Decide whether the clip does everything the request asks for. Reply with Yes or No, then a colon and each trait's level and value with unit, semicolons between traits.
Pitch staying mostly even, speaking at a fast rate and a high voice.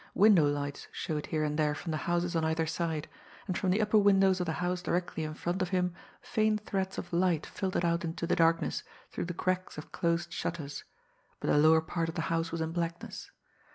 No: narrow, 2.3 semitones; fast, 220 wpm; medium, 170 Hz